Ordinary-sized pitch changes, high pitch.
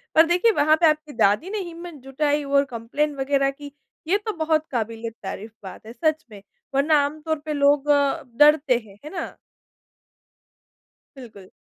Yes: average, 3.7 semitones; very high, 290 Hz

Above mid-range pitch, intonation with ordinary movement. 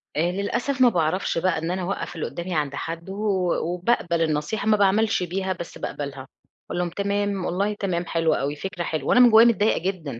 No: medium, 180 Hz; average, 3.5 semitones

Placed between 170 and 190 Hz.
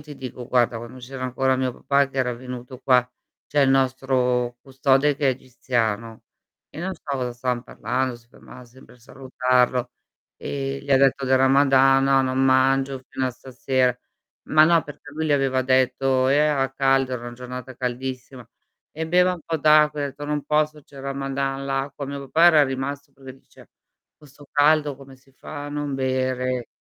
No: low, 135 Hz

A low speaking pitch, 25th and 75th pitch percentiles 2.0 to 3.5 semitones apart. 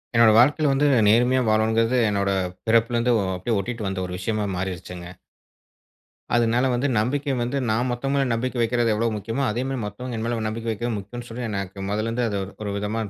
Yes: low, 115 Hz; average, 2.8 semitones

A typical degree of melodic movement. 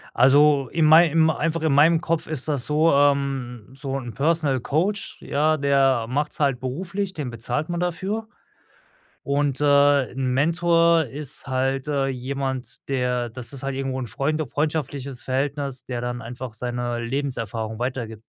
Yes: average, 3.4 semitones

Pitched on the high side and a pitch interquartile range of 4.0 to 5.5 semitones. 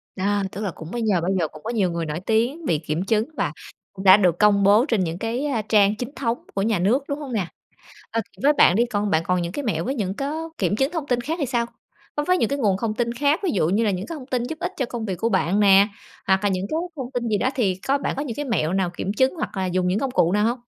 Yes: high, 215 Hz; average, 5.2 semitones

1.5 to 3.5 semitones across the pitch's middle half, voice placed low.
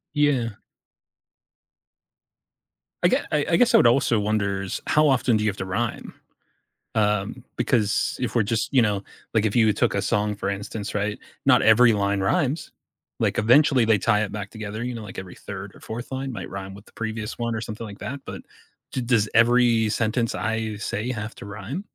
Yes: average, 2.8 semitones; low, 110 Hz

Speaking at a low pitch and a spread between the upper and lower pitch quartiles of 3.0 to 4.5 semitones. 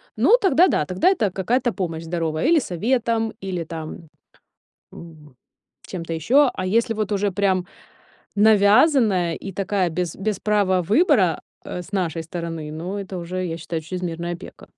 No: medium, 185 Hz; average, 4.2 semitones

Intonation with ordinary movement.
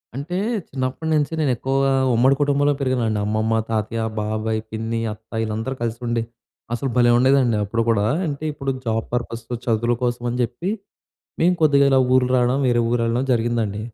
Yes: average, 3.1 semitones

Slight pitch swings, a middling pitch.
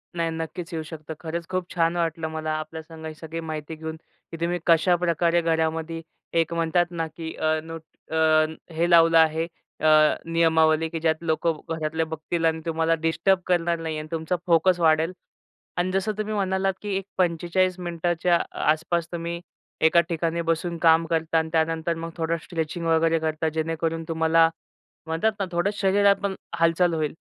Yes: narrow, 1.2 semitones; medium, 165 Hz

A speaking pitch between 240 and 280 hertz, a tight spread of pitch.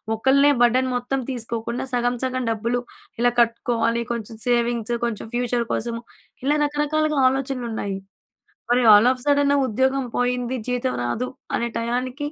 Yes: high, 245 Hz; narrow, 1.9 semitones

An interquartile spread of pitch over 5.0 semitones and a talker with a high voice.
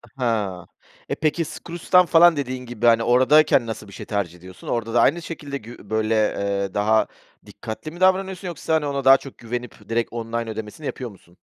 No: wide, 5.6 semitones; low, 120 Hz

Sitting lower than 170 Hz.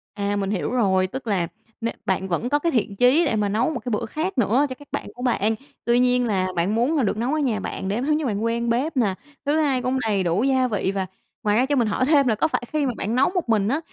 No: high, 235 Hz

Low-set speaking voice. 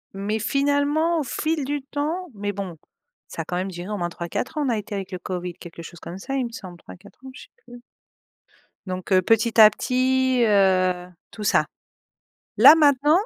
No: high, 215 Hz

